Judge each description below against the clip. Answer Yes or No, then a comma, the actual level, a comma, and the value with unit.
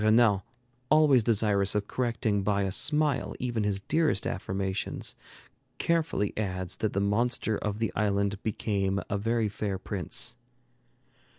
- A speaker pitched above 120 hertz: No, low, 105 Hz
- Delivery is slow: Yes, slow, 130 wpm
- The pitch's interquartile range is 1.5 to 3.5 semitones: Yes, average, 2.9 semitones